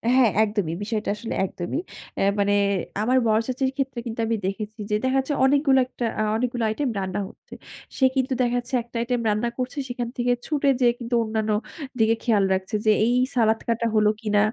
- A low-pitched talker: No, high, 235 Hz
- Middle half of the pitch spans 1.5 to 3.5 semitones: Yes, average, 3.0 semitones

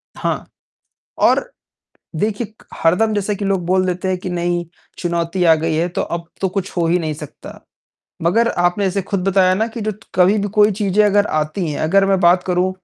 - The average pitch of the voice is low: No, medium, 185 Hz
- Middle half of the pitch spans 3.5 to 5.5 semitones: No, average, 2.8 semitones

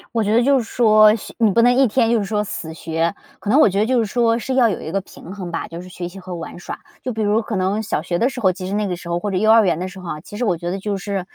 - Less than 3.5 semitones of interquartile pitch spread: No, average, 3.8 semitones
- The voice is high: Yes, high, 205 Hz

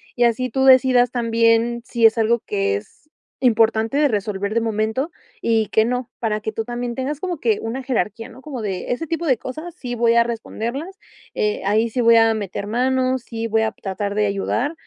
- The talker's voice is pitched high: Yes, high, 230 Hz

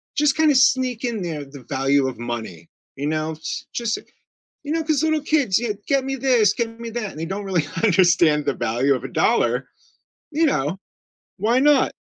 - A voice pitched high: Yes, high, 210 Hz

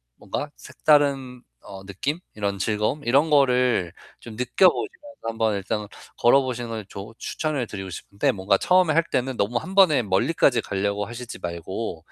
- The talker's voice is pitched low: Yes, low, 120 Hz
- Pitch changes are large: Yes, wide, 5.9 semitones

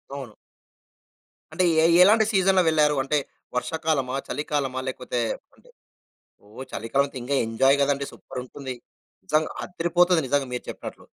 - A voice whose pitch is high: No, medium, 140 Hz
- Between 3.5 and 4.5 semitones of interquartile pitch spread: Yes, average, 3.9 semitones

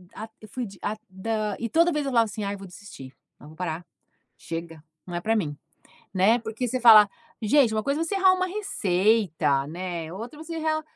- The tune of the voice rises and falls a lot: Yes, wide, 6.2 semitones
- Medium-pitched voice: No, high, 215 Hz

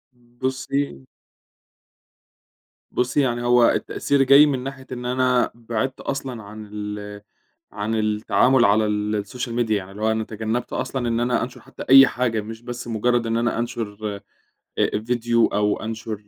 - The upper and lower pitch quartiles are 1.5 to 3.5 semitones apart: Yes, average, 2.7 semitones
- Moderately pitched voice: No, low, 115 Hz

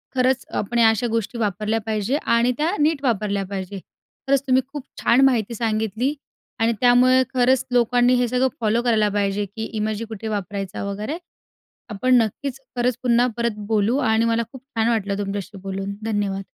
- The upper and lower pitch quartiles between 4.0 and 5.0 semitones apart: No, average, 3.3 semitones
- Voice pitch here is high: Yes, high, 225 Hz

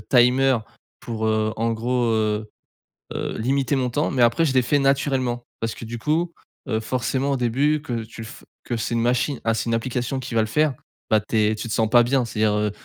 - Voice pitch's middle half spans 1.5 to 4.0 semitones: Yes, average, 3.0 semitones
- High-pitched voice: No, low, 120 Hz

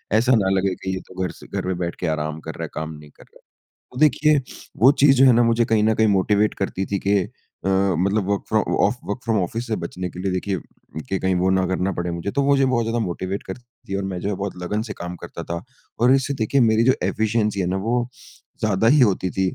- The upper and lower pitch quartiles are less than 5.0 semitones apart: Yes, average, 3.7 semitones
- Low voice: Yes, low, 100 Hz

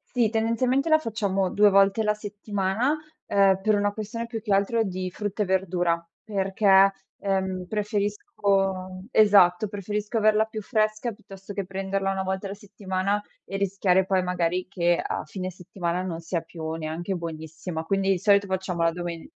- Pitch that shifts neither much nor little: No, narrow, 2.2 semitones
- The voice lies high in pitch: Yes, high, 195 Hz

